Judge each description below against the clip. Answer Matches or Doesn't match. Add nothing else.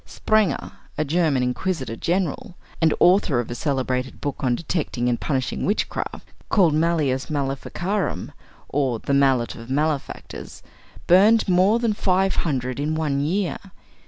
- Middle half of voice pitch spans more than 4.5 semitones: Matches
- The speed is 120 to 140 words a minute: Matches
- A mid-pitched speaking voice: Matches